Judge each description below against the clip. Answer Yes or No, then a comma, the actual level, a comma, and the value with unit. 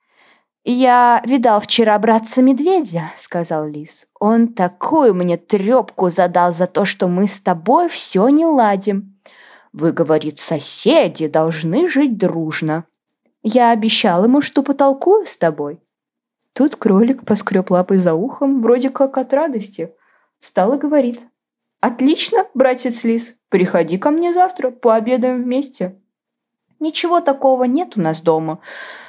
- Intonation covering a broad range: Yes, wide, 7.0 semitones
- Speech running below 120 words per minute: No, average, 130 wpm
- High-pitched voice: Yes, high, 230 Hz